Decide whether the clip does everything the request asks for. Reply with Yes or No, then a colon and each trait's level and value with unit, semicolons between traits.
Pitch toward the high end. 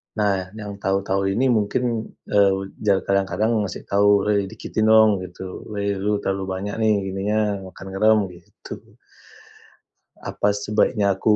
No: low, 100 Hz